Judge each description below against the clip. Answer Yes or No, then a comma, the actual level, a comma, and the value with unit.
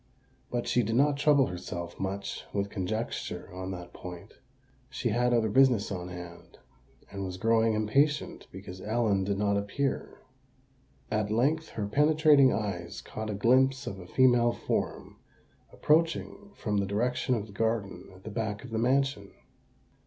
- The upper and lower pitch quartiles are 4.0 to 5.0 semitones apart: Yes, average, 4.5 semitones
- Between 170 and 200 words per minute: No, average, 155 wpm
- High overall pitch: No, low, 110 Hz